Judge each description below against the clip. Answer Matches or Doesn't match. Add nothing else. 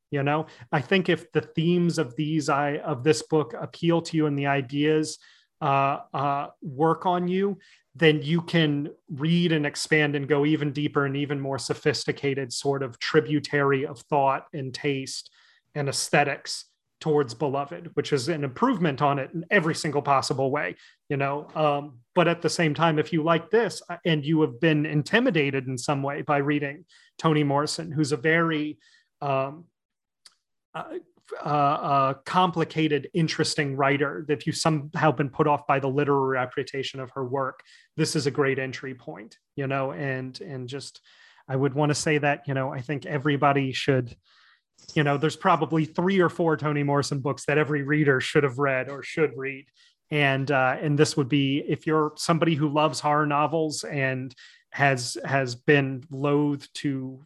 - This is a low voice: Doesn't match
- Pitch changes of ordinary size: Doesn't match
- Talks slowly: Doesn't match